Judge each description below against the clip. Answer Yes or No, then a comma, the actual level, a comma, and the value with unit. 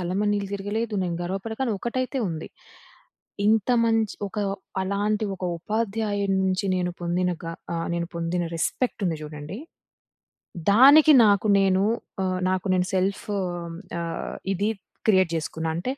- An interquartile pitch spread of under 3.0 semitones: No, average, 3.3 semitones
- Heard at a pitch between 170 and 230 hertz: Yes, high, 195 Hz